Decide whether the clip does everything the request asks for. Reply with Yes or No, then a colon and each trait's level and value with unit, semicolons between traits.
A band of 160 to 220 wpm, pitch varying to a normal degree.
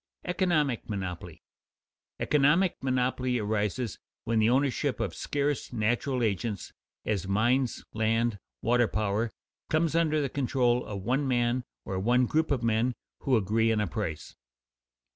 No: average, 140 wpm; average, 3.9 semitones